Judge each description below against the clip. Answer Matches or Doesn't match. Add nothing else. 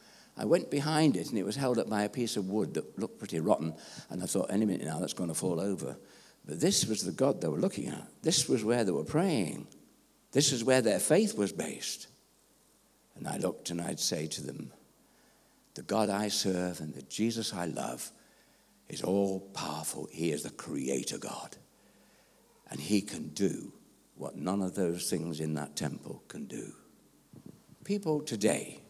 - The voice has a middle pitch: Doesn't match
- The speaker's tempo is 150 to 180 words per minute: Doesn't match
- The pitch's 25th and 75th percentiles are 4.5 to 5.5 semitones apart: Matches